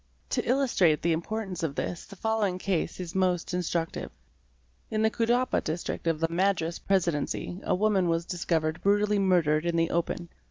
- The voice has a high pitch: No, medium, 180 Hz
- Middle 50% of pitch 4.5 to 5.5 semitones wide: No, average, 3.2 semitones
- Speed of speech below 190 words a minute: Yes, average, 165 wpm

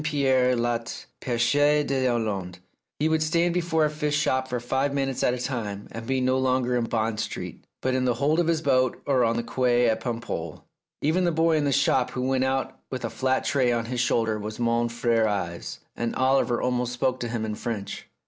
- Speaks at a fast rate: Yes, fast, 215 wpm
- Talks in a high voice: No, low, 125 Hz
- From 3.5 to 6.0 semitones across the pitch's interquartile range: No, average, 2.8 semitones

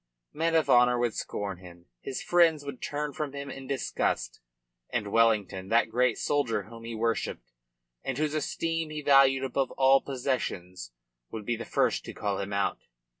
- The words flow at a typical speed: Yes, average, 175 wpm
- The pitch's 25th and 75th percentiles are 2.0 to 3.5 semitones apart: No, average, 4.9 semitones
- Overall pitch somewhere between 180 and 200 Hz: No, low, 125 Hz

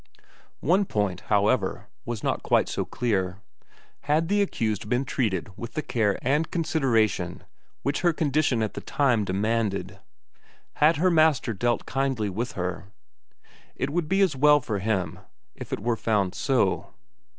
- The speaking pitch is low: Yes, low, 120 Hz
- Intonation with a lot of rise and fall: Yes, wide, 6.3 semitones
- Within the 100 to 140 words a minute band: No, average, 150 wpm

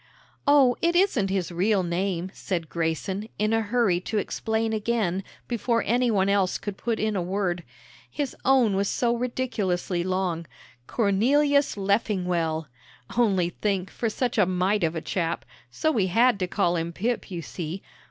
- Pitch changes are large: No, average, 4.5 semitones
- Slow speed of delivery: No, average, 160 wpm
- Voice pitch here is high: Yes, high, 200 Hz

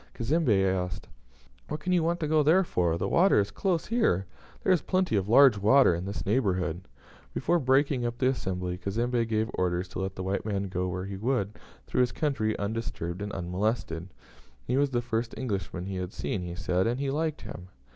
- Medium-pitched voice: No, low, 110 Hz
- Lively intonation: Yes, wide, 6.5 semitones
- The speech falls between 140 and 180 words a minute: No, fast, 205 wpm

